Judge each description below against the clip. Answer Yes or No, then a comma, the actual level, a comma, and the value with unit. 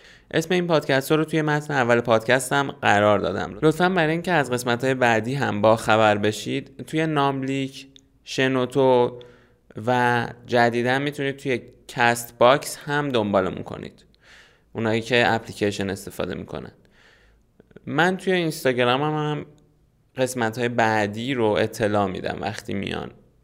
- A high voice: No, low, 125 Hz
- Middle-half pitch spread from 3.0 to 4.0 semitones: Yes, average, 3.4 semitones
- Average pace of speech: Yes, average, 135 wpm